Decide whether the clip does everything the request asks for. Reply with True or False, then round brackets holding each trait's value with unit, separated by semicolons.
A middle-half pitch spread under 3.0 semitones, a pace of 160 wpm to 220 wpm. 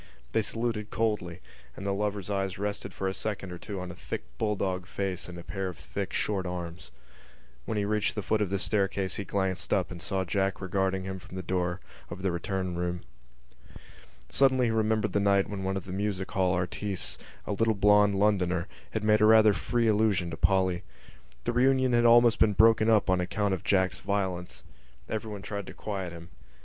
True (2.4 semitones; 200 wpm)